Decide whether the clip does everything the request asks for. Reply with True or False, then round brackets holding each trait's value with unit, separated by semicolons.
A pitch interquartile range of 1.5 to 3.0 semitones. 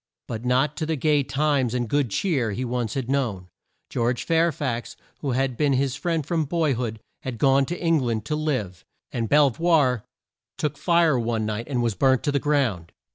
False (4.2 semitones)